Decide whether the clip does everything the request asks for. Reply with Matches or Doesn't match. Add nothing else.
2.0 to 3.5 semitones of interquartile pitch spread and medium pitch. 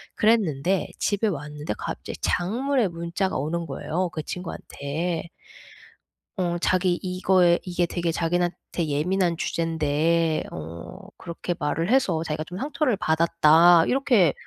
Matches